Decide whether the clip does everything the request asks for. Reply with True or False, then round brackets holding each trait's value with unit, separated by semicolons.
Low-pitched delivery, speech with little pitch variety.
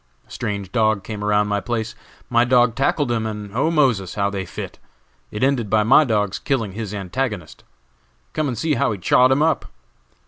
False (110 Hz; 4.0 semitones)